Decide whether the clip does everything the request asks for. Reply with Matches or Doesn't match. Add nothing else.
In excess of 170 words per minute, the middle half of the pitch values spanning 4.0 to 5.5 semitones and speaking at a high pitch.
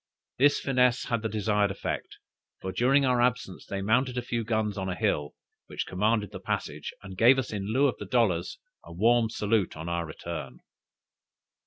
Doesn't match